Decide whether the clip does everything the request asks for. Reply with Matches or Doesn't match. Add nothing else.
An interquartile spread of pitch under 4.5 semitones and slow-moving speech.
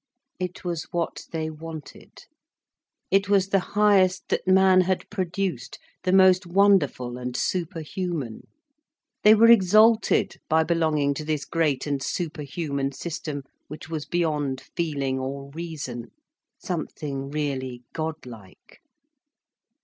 Doesn't match